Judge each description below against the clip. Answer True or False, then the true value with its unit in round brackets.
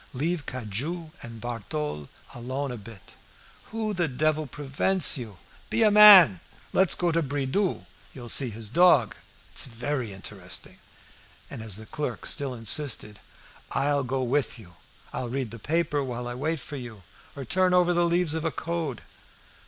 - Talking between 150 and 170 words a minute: True (160 wpm)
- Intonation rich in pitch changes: True (6.0 semitones)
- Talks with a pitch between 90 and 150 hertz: True (135 Hz)